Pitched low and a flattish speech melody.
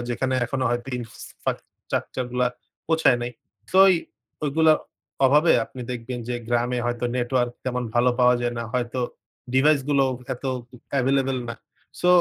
Yes: low, 125 Hz; narrow, 2.0 semitones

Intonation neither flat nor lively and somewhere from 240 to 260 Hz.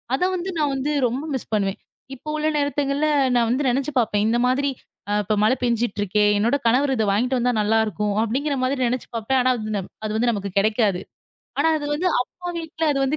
Yes: average, 4.7 semitones; high, 245 Hz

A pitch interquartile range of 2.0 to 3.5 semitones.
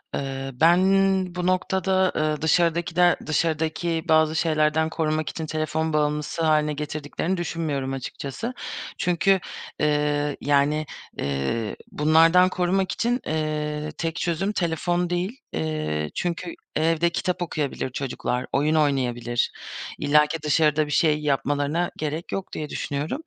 Yes: average, 2.9 semitones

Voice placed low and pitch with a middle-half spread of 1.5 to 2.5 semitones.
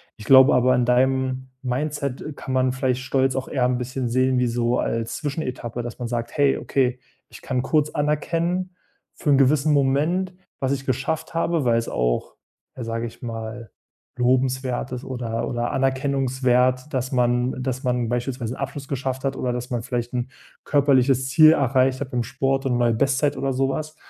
Yes: low, 130 Hz; narrow, 1.9 semitones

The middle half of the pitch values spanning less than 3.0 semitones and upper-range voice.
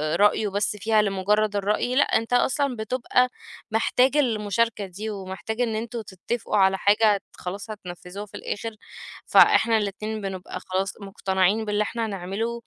Yes: narrow, 2.5 semitones; high, 210 Hz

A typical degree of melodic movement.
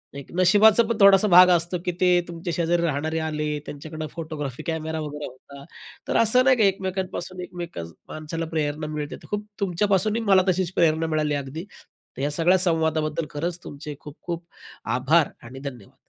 Yes: average, 3.3 semitones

